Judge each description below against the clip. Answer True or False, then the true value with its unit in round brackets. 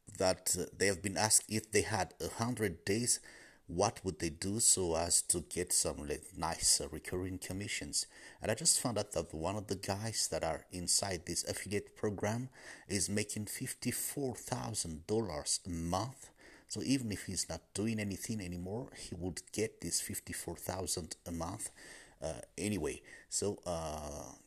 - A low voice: True (95 Hz)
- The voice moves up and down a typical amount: True (3.5 semitones)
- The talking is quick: False (160 wpm)